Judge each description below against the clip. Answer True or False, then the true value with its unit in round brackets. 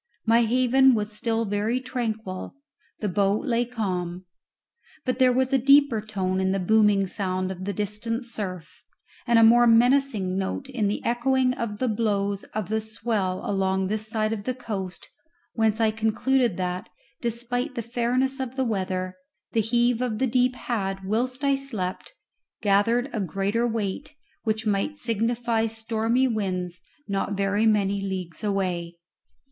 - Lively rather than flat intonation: False (3.6 semitones)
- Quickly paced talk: False (155 wpm)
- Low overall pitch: False (220 Hz)